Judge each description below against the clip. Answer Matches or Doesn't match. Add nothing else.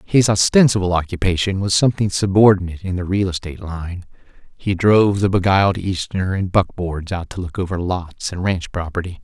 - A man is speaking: Matches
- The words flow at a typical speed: Matches